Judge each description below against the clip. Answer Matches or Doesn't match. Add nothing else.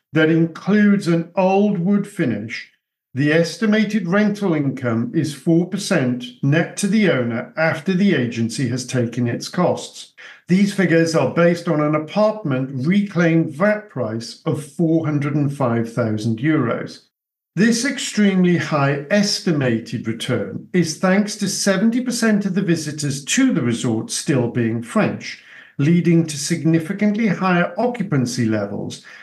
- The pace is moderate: Doesn't match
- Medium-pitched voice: Matches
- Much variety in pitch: Matches